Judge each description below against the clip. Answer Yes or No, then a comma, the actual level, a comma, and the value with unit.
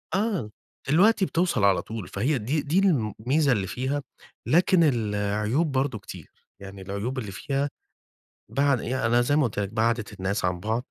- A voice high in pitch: No, low, 120 Hz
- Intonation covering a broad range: Yes, wide, 5.8 semitones